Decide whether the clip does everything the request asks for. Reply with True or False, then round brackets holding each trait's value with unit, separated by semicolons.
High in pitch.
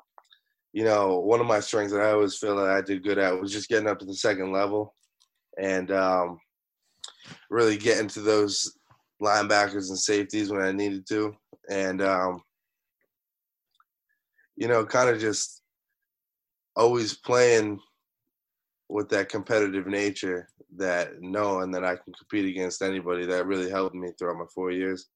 False (100 Hz)